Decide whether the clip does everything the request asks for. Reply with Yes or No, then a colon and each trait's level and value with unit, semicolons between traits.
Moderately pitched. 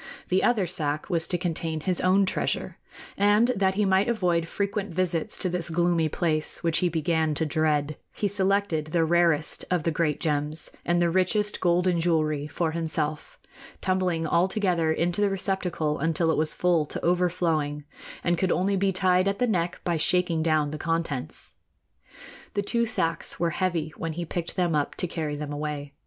Yes: medium, 170 Hz